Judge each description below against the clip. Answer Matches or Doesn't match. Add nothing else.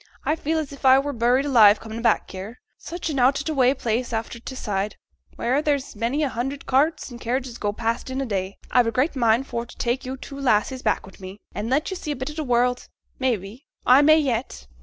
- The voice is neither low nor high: Doesn't match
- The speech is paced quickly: Matches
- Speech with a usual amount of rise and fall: Matches